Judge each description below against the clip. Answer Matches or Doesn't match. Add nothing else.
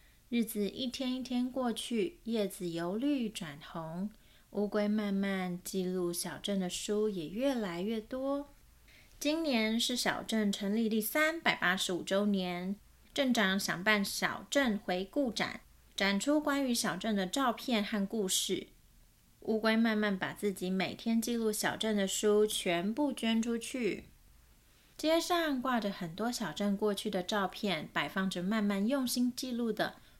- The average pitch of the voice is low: Doesn't match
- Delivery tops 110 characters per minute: Matches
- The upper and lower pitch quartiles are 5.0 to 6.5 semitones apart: Doesn't match